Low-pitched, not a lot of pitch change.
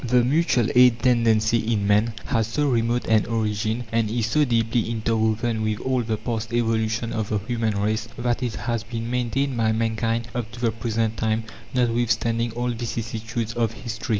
Yes: low, 115 Hz; narrow, 1.4 semitones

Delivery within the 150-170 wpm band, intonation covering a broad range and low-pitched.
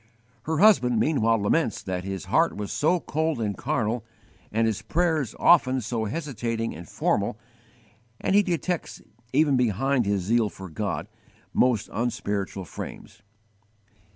No: slow, 135 wpm; wide, 6.5 semitones; low, 115 Hz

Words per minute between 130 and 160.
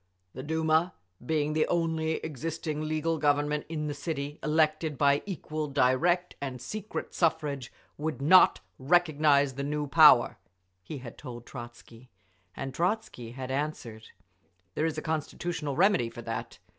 Yes: average, 140 wpm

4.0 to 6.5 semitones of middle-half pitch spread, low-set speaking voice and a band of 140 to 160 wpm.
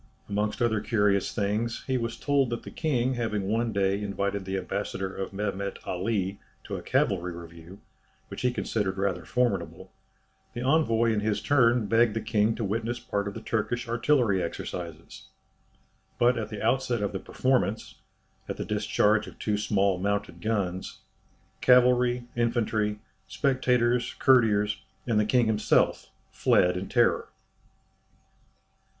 No: average, 3.1 semitones; low, 110 Hz; average, 145 wpm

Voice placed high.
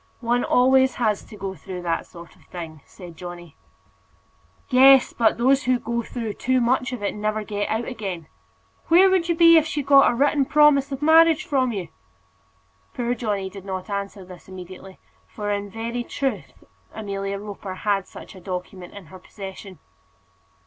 Yes: high, 215 Hz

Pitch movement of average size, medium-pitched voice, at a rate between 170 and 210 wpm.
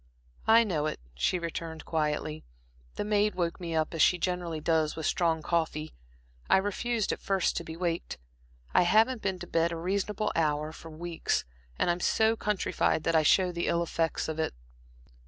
Yes: average, 3.1 semitones; medium, 170 Hz; average, 190 wpm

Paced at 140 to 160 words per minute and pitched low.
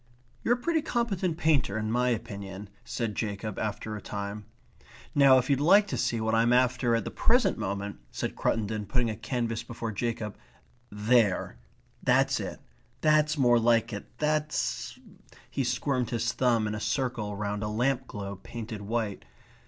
No: average, 170 wpm; low, 115 Hz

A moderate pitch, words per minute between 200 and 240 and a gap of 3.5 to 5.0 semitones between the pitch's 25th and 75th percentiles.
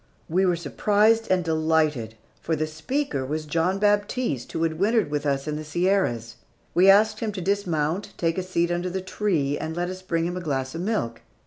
Yes: medium, 170 Hz; fast, 205 wpm; average, 4.1 semitones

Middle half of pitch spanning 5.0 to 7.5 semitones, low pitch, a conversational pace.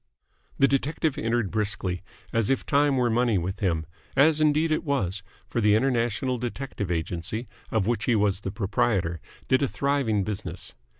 Yes: wide, 5.6 semitones; low, 115 Hz; average, 165 wpm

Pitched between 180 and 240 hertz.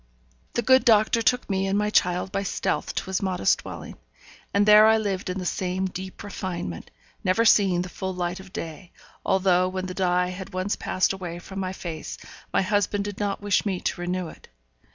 Yes: high, 190 Hz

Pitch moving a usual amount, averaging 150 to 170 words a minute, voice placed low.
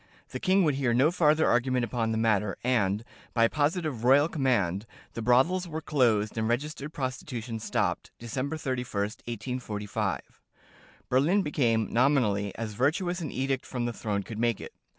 Yes: average, 4.5 semitones; average, 160 wpm; low, 125 Hz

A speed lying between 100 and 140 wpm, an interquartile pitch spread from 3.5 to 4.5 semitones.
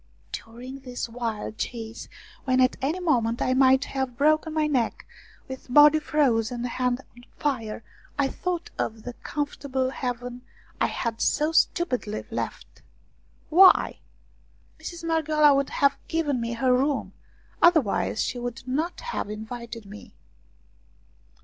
Yes: slow, 135 wpm; average, 3.9 semitones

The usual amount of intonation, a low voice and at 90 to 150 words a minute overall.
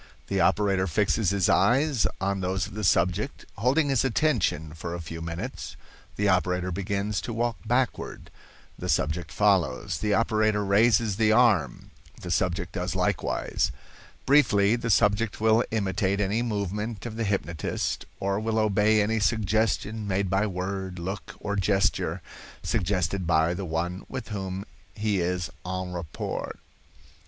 Yes: average, 3.1 semitones; low, 100 Hz; average, 145 wpm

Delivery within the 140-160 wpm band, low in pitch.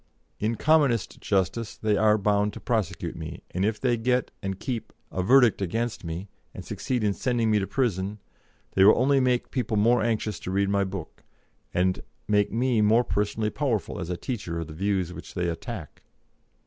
No: average, 185 wpm; low, 105 Hz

